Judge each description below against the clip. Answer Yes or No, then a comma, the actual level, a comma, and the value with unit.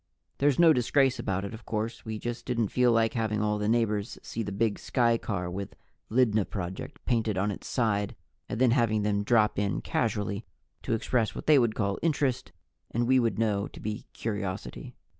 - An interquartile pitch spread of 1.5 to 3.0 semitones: Yes, narrow, 2.6 semitones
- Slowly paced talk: No, average, 190 wpm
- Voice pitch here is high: No, low, 110 Hz